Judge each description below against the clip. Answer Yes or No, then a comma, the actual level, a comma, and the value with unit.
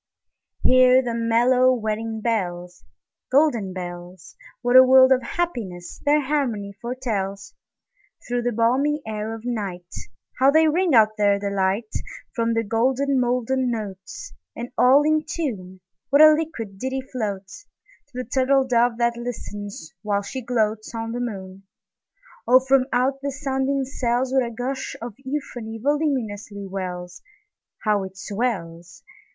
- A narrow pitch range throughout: No, average, 4.5 semitones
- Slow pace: Yes, slow, 115 wpm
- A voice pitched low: No, high, 235 Hz